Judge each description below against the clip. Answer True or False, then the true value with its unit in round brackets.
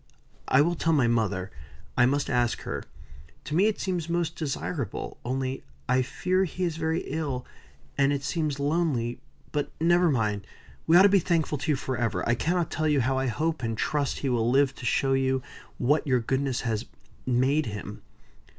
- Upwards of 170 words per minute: True (185 wpm)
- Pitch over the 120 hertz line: True (140 Hz)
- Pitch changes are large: False (4.6 semitones)